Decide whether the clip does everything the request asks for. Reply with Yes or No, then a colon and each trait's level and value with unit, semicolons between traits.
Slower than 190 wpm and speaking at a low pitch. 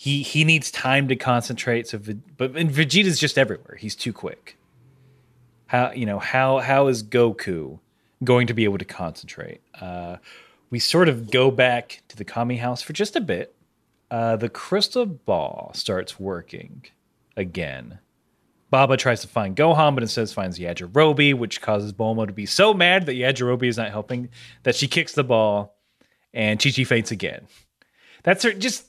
Yes: average, 175 wpm; low, 125 Hz